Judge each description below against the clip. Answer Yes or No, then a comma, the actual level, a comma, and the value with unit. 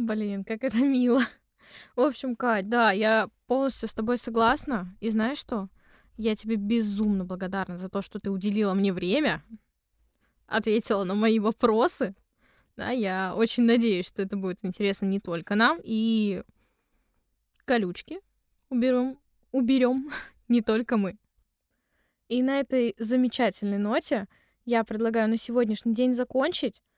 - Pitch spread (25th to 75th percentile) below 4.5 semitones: Yes, average, 3.4 semitones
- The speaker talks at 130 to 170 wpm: Yes, average, 135 wpm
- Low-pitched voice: No, high, 225 Hz